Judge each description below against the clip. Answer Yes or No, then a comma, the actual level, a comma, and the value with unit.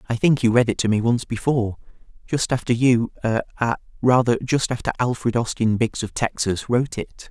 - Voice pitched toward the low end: Yes, low, 120 Hz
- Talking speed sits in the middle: Yes, average, 165 wpm